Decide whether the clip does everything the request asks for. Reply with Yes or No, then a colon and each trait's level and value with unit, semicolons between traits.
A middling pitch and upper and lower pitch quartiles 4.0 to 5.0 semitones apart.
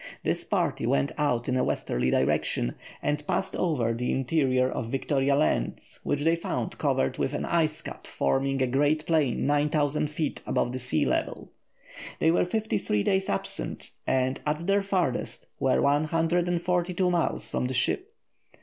Yes: medium, 145 Hz; average, 4.6 semitones